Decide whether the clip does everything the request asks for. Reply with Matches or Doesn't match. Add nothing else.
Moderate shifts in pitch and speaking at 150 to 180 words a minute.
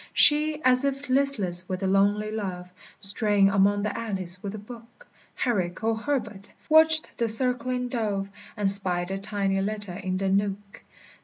Matches